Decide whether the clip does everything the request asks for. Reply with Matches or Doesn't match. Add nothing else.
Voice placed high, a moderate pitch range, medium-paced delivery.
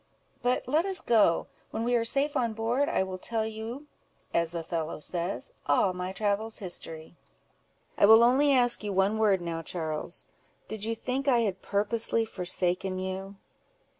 Matches